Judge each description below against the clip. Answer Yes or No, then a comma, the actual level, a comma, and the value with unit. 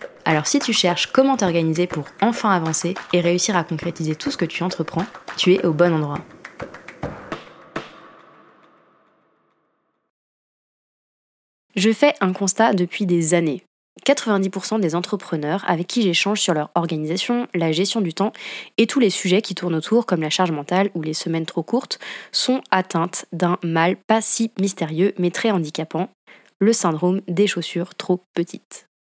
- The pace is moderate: Yes, average, 155 wpm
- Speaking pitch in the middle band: Yes, medium, 180 Hz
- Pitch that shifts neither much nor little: Yes, average, 3.5 semitones